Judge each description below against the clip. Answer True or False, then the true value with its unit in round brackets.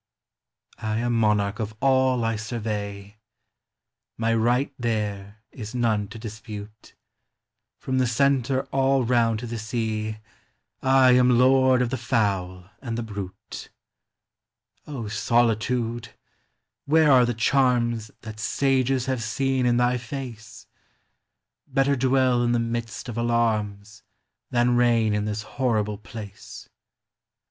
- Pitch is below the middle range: True (115 Hz)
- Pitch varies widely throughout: False (2.7 semitones)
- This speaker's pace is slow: True (125 wpm)